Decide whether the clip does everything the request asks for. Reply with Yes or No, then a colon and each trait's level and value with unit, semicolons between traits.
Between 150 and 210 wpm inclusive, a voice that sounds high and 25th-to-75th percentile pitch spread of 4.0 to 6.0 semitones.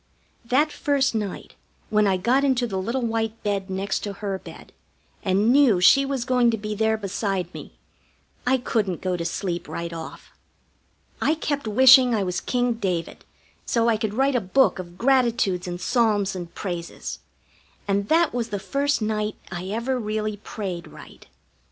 Yes: average, 170 wpm; high, 215 Hz; average, 4.5 semitones